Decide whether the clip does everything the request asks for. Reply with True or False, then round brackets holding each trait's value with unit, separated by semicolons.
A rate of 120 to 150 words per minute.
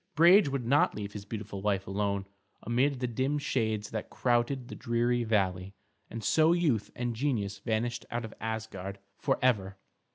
False (160 wpm)